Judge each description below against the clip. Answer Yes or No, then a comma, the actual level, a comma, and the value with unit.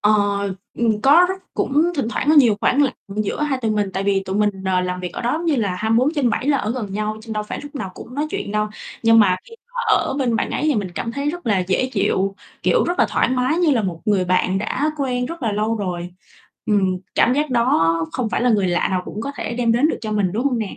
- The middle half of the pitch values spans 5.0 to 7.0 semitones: Yes, wide, 5.4 semitones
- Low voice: No, high, 225 Hz